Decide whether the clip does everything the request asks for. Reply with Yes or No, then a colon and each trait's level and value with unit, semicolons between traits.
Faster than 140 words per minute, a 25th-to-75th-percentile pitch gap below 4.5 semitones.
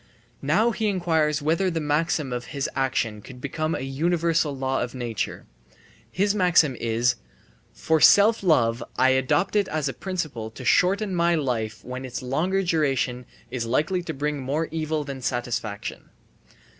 No: average, 155 wpm; average, 5.0 semitones